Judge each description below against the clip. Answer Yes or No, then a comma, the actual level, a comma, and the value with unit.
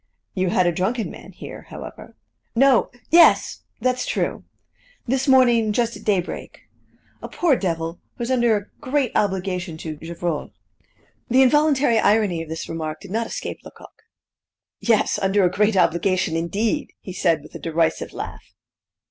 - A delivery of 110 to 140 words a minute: No, average, 155 wpm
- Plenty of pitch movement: Yes, wide, 5.9 semitones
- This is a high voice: Yes, high, 205 Hz